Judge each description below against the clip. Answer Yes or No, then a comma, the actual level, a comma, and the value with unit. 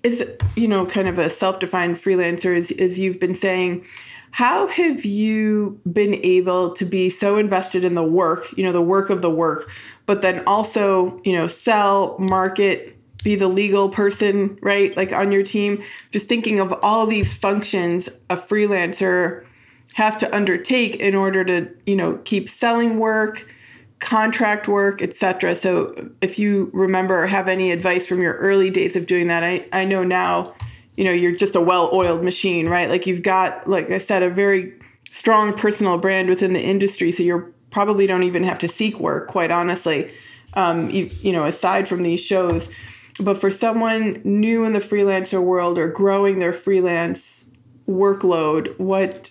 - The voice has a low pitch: No, high, 190 Hz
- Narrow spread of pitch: Yes, narrow, 2.2 semitones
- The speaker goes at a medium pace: Yes, average, 175 wpm